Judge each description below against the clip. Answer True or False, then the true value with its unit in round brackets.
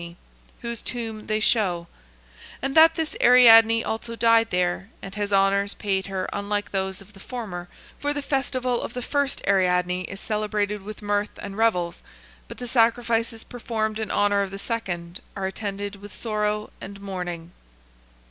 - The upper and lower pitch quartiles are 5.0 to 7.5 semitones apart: False (2.9 semitones)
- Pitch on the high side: True (210 Hz)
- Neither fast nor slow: True (165 wpm)